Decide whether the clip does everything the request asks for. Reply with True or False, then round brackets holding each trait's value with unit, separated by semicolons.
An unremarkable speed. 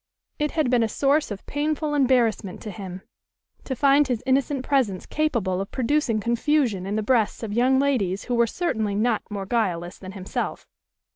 True (180 wpm)